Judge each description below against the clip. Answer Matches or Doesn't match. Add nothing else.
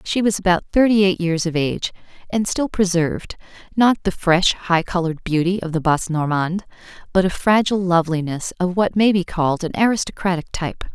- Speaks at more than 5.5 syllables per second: Matches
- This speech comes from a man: Doesn't match